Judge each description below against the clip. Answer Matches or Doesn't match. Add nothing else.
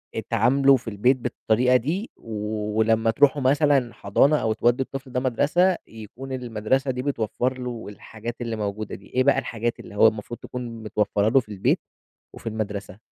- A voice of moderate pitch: Doesn't match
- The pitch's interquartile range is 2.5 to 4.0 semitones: Matches